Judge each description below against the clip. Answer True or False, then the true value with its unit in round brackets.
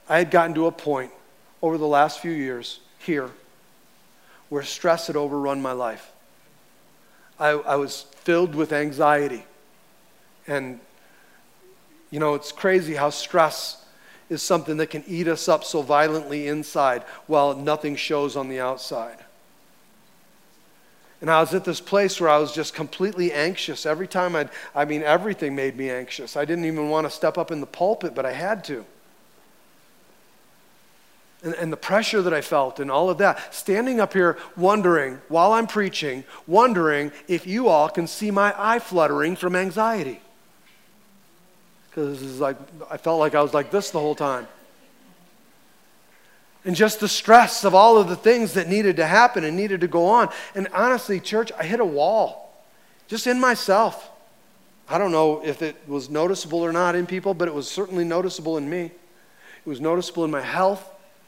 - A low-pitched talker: False (165 Hz)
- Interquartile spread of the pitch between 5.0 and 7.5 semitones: False (4.4 semitones)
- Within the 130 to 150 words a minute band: False (170 wpm)